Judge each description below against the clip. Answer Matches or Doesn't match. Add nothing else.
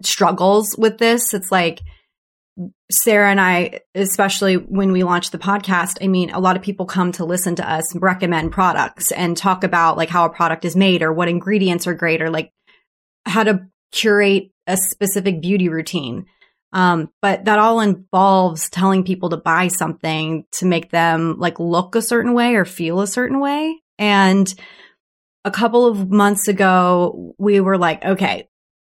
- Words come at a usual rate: Matches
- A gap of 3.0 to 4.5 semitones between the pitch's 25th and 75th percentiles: Doesn't match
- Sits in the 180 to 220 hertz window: Matches